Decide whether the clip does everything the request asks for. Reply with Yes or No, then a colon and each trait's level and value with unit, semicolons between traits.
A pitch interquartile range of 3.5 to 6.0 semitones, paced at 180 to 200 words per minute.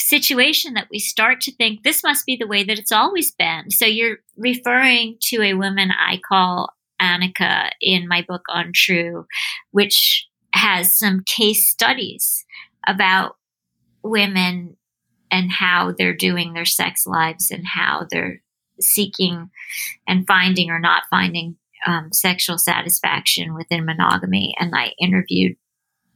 No: average, 4.0 semitones; average, 140 wpm